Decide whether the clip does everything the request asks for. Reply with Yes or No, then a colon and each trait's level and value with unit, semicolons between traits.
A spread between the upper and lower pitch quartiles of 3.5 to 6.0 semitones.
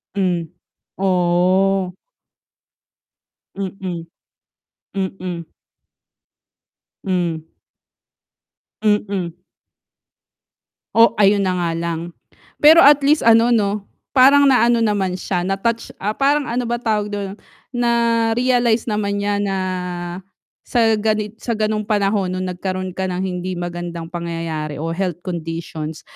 Yes: average, 4.1 semitones